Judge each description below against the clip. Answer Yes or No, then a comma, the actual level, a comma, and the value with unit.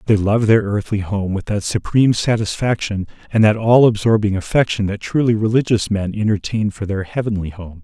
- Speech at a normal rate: Yes, average, 175 wpm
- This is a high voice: No, low, 105 Hz